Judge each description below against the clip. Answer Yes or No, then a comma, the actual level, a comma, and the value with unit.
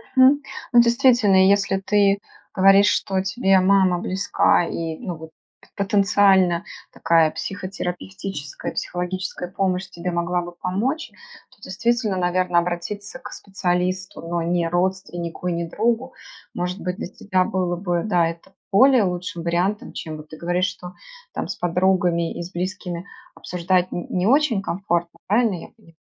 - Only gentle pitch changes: Yes, narrow, 2.2 semitones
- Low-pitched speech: No, medium, 185 Hz